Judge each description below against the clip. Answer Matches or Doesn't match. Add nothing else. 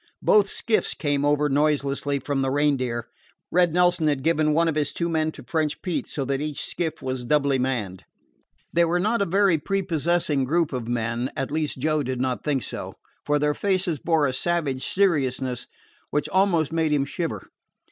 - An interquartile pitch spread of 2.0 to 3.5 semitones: Doesn't match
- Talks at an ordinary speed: Matches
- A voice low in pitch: Doesn't match